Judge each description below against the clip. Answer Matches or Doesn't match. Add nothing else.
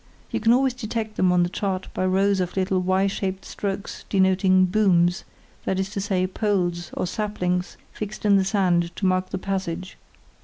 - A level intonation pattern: Matches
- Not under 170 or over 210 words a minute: Matches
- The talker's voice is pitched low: Doesn't match